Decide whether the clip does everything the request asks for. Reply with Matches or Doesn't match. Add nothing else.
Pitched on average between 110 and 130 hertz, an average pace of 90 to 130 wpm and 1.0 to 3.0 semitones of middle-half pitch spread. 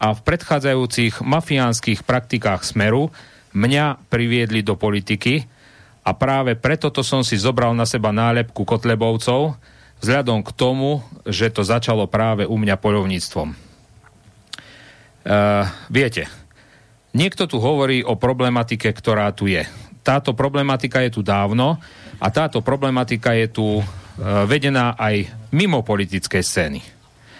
Doesn't match